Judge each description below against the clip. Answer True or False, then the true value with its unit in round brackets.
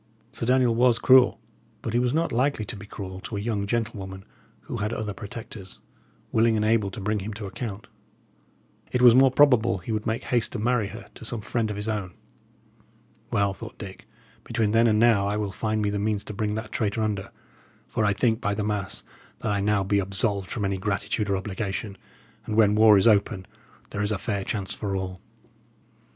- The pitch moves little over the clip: True (2.3 semitones)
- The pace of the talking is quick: True (210 wpm)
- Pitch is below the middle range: True (105 Hz)